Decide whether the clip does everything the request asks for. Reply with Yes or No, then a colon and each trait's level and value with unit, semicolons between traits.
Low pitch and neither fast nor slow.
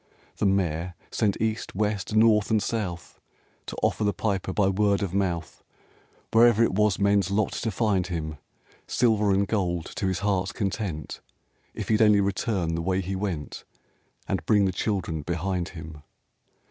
Yes: low, 100 Hz; average, 160 wpm